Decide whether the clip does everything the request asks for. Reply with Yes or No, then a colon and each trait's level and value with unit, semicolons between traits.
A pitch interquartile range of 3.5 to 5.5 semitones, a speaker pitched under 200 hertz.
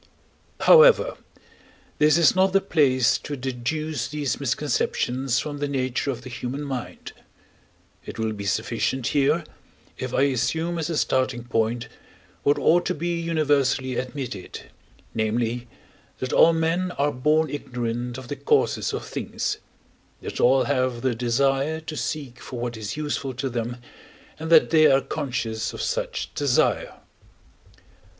Yes: average, 3.9 semitones; low, 135 Hz